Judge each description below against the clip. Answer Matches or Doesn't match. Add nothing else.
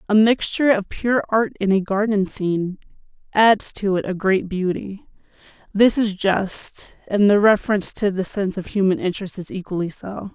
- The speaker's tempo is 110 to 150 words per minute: Doesn't match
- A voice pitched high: Matches